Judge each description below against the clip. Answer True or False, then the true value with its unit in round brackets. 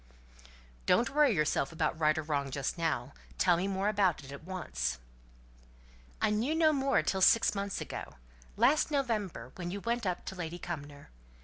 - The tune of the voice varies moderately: False (5.9 semitones)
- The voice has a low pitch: False (180 Hz)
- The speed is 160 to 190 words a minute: True (175 wpm)